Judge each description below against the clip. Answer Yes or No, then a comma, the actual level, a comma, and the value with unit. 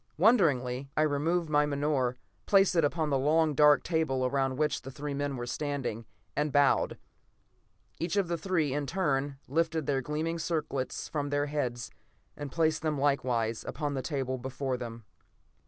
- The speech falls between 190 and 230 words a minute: No, average, 165 wpm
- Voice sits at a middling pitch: Yes, medium, 145 Hz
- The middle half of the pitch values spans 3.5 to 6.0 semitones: No, average, 2.9 semitones